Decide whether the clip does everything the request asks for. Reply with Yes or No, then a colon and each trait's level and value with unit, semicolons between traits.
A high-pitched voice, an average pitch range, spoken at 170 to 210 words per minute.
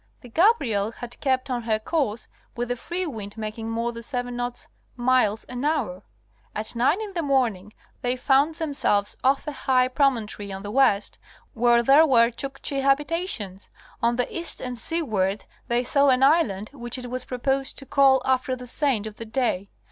Yes: very high, 250 Hz; average, 3.5 semitones; average, 185 wpm